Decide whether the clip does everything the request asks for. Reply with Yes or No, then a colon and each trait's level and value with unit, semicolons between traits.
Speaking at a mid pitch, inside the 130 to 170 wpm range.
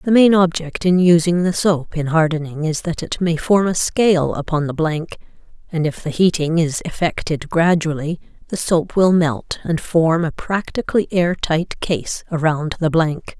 No: medium, 165 Hz; average, 180 wpm